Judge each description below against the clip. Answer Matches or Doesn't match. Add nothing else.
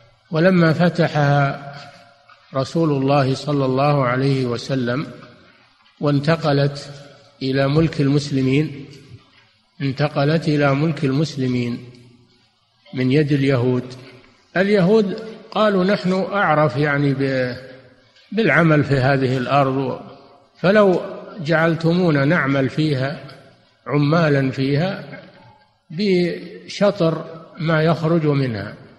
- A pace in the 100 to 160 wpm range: Doesn't match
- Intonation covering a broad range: Doesn't match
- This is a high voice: Doesn't match